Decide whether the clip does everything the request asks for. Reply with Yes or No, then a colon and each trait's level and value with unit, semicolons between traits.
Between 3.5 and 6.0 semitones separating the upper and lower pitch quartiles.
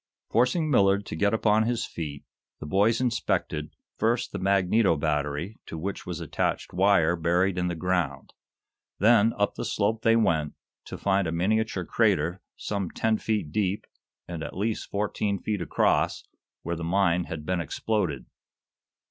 Yes: average, 4.4 semitones